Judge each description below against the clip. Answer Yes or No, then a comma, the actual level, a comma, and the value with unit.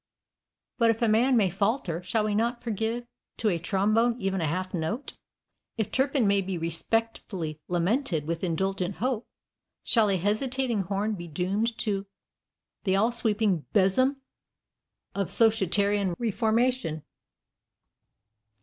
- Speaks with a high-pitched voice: Yes, high, 205 Hz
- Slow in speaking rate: Yes, slow, 130 wpm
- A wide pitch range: No, average, 3.8 semitones